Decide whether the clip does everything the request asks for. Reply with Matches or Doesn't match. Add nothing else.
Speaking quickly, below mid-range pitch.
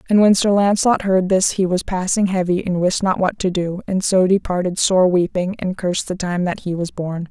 Doesn't match